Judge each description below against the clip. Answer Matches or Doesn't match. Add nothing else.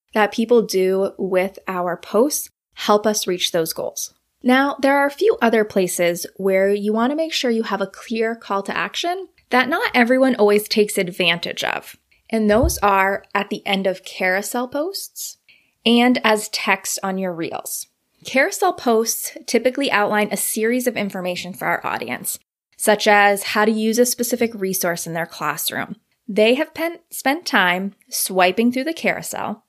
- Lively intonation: Doesn't match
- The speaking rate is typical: Matches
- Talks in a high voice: Matches